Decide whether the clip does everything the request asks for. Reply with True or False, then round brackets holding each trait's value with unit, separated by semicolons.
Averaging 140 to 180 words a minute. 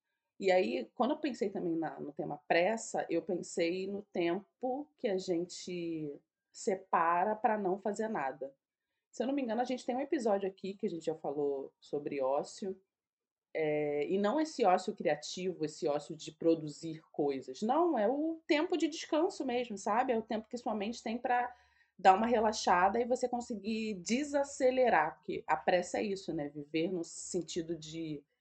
True (175 wpm)